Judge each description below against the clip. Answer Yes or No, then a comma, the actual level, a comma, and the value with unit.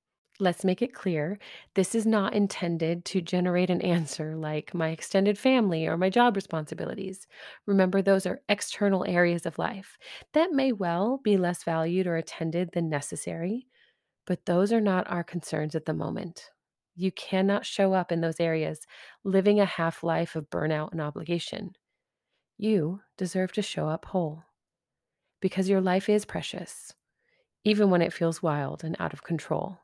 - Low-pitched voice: No, medium, 180 Hz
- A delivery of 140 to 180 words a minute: Yes, average, 165 wpm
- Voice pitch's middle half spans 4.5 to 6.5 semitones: No, average, 3.3 semitones